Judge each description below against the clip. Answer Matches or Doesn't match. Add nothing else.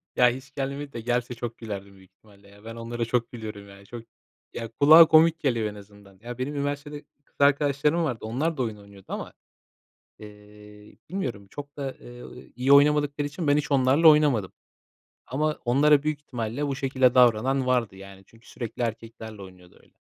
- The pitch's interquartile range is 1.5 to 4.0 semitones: Doesn't match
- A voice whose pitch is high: Doesn't match